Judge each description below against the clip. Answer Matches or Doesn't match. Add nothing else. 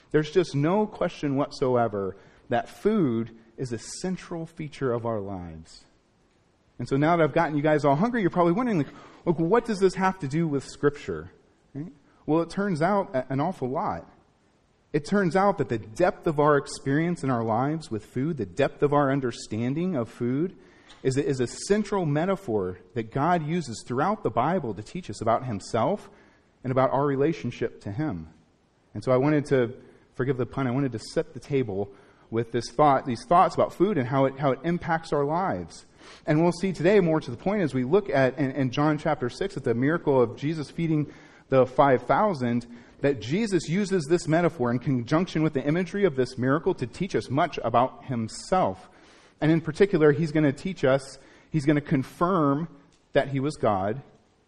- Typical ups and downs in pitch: Matches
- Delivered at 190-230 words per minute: Matches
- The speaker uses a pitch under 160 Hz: Matches